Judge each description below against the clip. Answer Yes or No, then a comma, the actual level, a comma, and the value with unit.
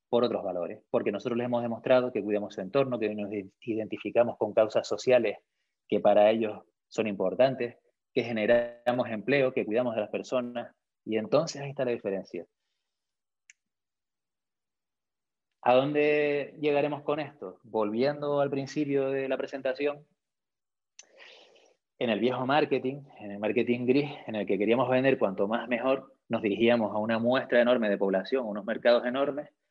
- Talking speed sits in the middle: Yes, average, 155 wpm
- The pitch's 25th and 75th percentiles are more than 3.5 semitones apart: Yes, average, 4.1 semitones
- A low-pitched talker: Yes, low, 125 Hz